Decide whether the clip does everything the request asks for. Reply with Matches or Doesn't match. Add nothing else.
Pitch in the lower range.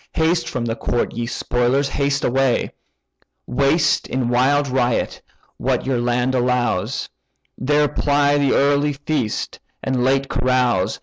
Matches